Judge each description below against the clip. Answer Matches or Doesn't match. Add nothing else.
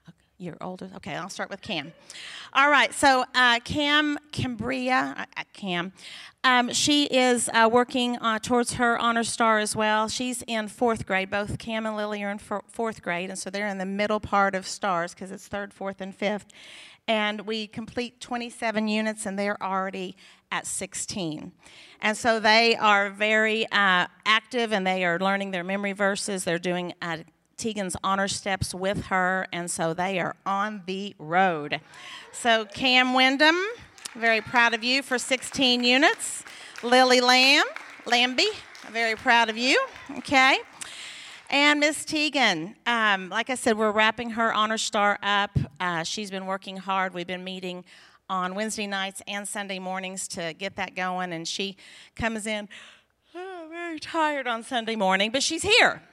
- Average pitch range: Matches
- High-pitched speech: Matches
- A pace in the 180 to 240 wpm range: Doesn't match